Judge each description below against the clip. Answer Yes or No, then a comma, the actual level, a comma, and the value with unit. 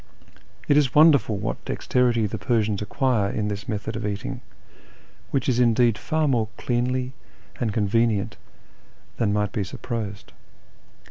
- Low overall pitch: Yes, low, 115 Hz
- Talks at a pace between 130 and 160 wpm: Yes, average, 140 wpm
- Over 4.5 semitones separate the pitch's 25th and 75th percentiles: No, average, 3.4 semitones